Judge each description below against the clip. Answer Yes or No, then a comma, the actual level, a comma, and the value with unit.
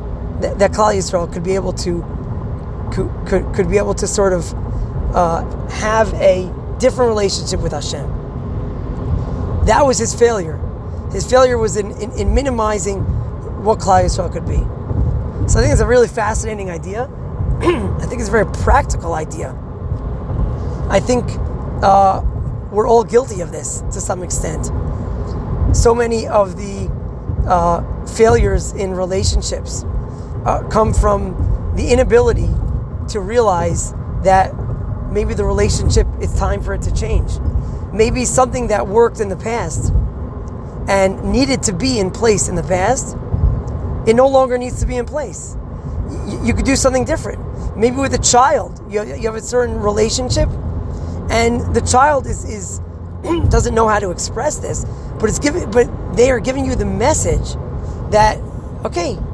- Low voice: No, high, 205 Hz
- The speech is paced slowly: No, average, 155 wpm